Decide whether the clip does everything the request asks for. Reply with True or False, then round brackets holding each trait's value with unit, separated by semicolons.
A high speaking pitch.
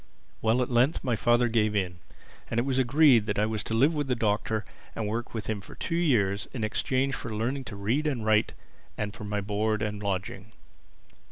False (110 Hz)